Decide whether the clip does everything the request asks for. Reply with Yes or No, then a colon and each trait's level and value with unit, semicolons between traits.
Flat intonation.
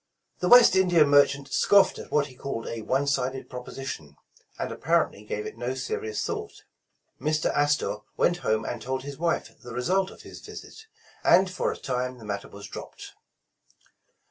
No: average, 4.1 semitones